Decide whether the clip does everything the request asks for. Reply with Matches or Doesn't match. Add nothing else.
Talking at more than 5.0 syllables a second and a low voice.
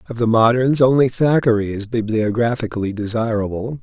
Matches